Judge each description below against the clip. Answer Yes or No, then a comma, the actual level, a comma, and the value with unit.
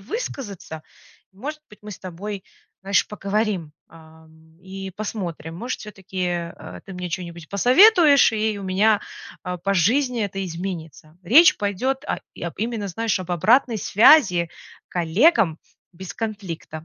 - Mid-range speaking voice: No, high, 195 Hz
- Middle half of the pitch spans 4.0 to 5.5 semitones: Yes, average, 4.4 semitones